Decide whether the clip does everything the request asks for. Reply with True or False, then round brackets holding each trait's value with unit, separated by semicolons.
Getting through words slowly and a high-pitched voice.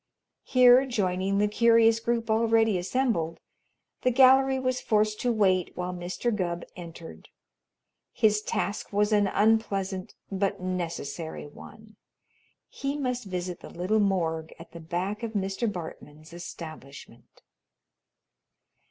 True (120 wpm; 200 Hz)